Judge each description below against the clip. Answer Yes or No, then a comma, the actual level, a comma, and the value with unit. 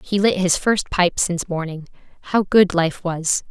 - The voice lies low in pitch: No, medium, 180 Hz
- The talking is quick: No, average, 190 wpm